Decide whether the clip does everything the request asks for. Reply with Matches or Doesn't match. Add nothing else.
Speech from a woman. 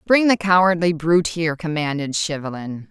Matches